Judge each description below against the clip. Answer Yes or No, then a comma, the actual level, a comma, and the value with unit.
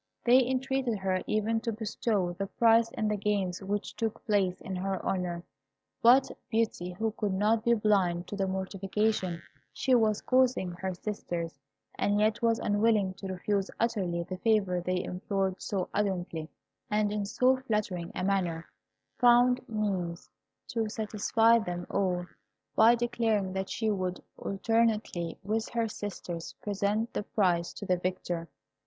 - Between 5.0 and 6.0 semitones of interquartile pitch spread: No, average, 3.4 semitones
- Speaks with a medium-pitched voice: No, high, 205 Hz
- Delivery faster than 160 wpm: No, average, 150 wpm